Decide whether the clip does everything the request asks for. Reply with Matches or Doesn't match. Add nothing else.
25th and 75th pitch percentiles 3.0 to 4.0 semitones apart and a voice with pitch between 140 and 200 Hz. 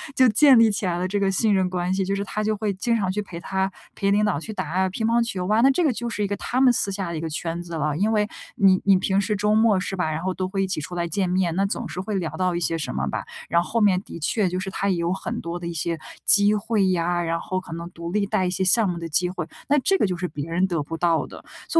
Matches